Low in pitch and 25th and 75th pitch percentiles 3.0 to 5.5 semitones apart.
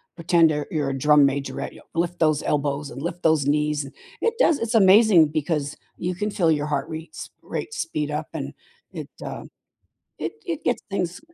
No: medium, 155 Hz; average, 3.5 semitones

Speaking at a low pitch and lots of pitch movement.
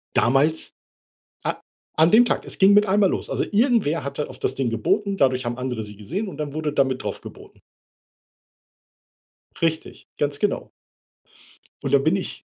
No: medium, 150 Hz; wide, 6.6 semitones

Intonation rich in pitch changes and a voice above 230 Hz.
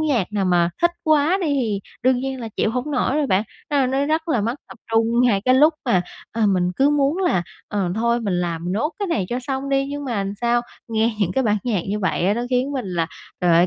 Yes: wide, 5.7 semitones; high, 240 Hz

